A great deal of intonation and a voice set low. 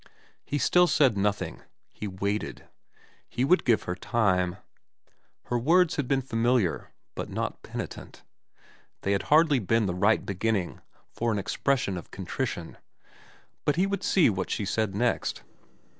Yes: wide, 5.9 semitones; low, 115 Hz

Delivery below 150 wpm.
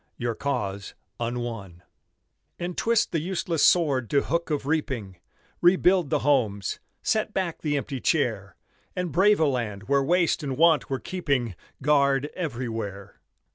Yes: average, 140 wpm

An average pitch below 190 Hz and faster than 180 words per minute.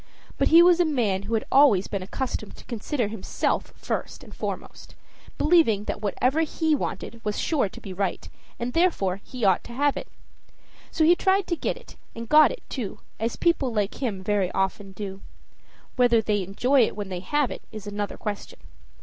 No: high, 225 Hz; average, 190 wpm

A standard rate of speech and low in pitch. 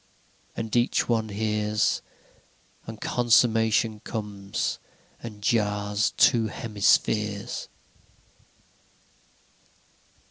No: slow, 65 wpm; low, 110 Hz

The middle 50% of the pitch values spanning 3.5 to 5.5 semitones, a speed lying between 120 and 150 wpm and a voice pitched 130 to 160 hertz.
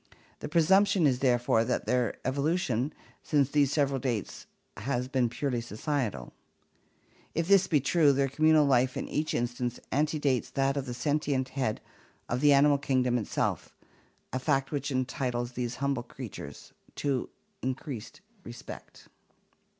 No: average, 2.9 semitones; average, 140 wpm; low, 135 Hz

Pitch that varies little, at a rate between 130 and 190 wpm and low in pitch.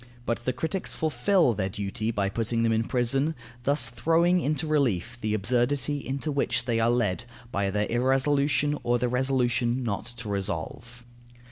No: average, 3.8 semitones; average, 160 wpm; low, 120 Hz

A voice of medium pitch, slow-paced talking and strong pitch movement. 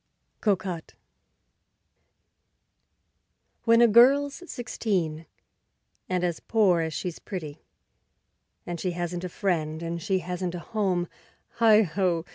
No: medium, 180 Hz; slow, 110 wpm; average, 3.7 semitones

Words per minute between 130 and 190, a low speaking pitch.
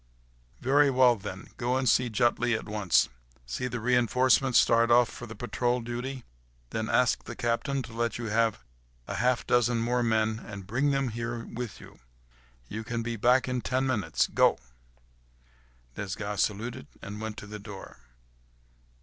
Yes: average, 165 wpm; low, 120 Hz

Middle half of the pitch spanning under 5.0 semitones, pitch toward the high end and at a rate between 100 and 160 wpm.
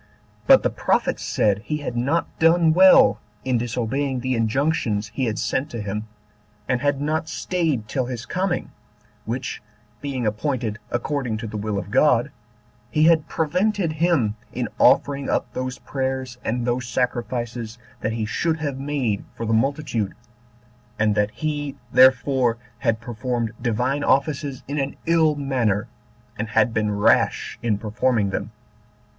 No: average, 4.4 semitones; low, 125 Hz; average, 150 wpm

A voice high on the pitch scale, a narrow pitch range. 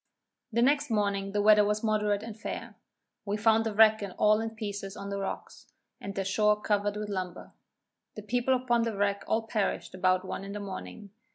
Yes: high, 210 Hz; narrow, 1.8 semitones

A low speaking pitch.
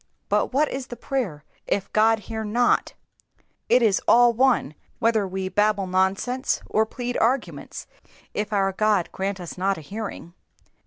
No: high, 215 Hz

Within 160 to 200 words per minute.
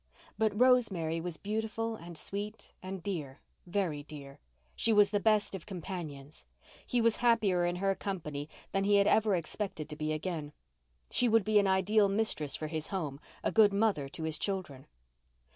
Yes: average, 170 wpm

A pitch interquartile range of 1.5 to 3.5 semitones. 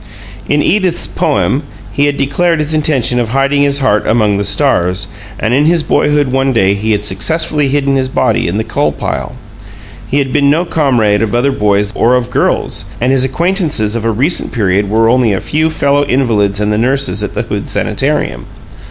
No: average, 5.3 semitones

